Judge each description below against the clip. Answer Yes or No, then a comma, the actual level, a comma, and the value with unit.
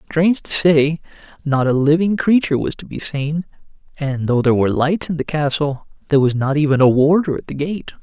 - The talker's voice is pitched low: No, medium, 150 Hz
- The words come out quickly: Yes, fast, 210 wpm